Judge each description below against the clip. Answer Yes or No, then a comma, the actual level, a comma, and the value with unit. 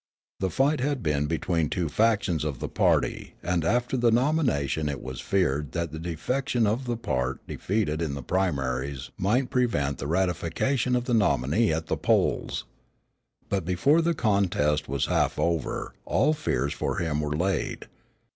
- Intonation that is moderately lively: No, wide, 8.0 semitones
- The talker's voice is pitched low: Yes, very low, 90 Hz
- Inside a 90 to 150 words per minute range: No, average, 165 wpm